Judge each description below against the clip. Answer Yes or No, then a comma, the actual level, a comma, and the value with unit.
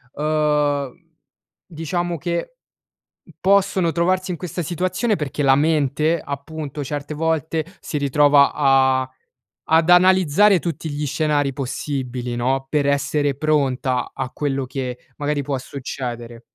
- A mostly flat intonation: No, average, 3.2 semitones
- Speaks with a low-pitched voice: No, medium, 145 Hz